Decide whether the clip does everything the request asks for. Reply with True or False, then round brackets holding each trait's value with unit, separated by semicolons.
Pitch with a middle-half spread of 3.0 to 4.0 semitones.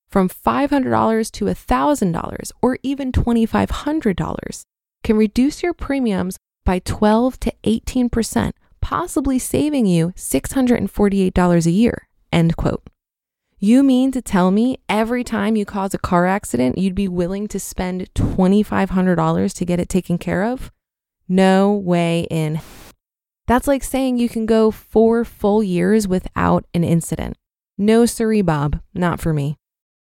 False (4.9 semitones)